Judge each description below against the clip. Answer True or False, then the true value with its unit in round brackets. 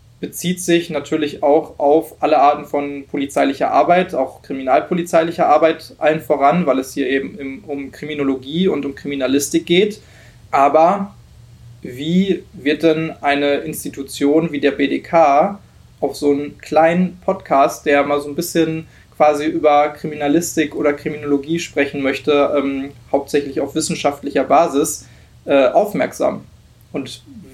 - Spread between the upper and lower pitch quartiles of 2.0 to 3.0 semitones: True (2.4 semitones)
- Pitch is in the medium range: True (145 Hz)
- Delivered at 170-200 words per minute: False (130 wpm)